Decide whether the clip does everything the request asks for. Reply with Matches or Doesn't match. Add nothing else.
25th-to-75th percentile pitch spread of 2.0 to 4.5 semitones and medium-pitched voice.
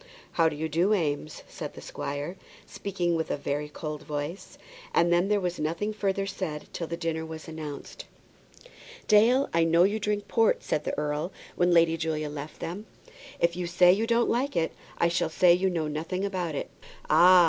Matches